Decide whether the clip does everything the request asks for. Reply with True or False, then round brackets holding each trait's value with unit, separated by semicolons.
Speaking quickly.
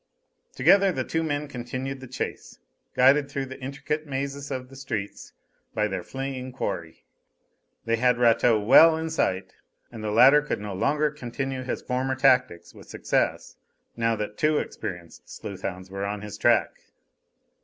False (160 wpm)